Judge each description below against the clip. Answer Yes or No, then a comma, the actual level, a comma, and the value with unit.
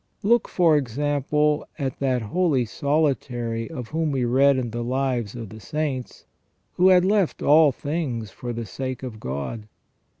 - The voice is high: No, low, 135 Hz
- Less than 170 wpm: Yes, average, 160 wpm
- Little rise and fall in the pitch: No, average, 4.2 semitones